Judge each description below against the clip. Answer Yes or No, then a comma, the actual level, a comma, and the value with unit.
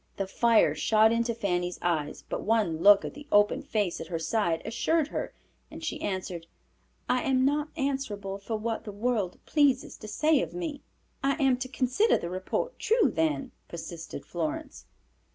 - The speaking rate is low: No, average, 175 wpm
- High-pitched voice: Yes, high, 220 Hz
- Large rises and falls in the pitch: Yes, wide, 6.8 semitones